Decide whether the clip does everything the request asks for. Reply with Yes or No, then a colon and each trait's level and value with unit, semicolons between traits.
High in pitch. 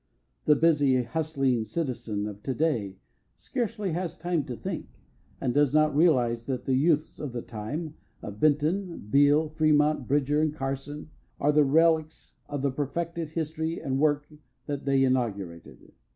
No: medium, 145 Hz